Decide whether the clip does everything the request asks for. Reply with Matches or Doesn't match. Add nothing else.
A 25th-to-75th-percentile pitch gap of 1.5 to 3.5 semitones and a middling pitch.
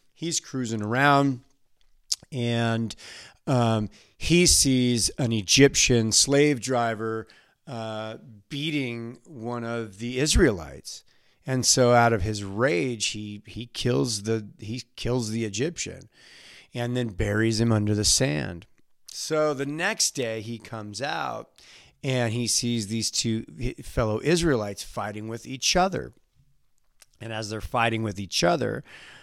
Doesn't match